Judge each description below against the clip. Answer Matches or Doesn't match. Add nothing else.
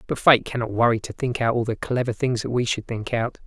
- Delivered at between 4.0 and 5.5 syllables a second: Doesn't match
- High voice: Doesn't match